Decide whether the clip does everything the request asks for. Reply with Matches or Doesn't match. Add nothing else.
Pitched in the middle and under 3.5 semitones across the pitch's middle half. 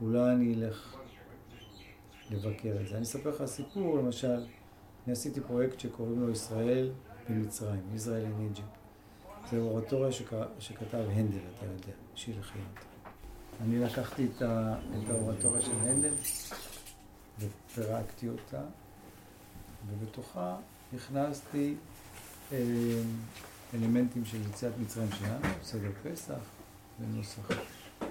Doesn't match